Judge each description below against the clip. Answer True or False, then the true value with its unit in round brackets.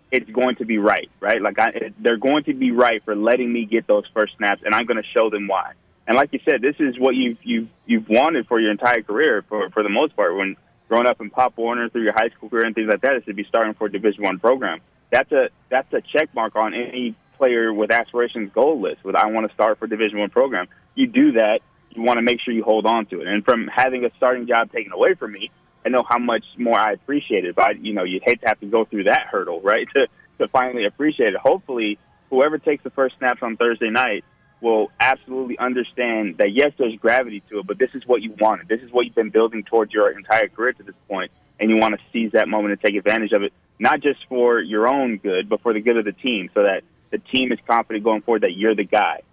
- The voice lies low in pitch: True (115 Hz)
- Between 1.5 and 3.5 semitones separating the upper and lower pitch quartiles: True (2.7 semitones)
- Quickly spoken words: True (265 wpm)